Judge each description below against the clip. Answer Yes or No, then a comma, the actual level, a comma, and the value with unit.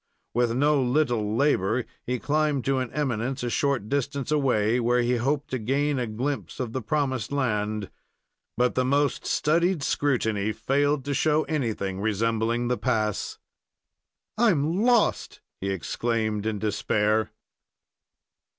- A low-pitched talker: Yes, low, 125 Hz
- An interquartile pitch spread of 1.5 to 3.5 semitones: No, average, 4.5 semitones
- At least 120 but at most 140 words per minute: Yes, slow, 135 wpm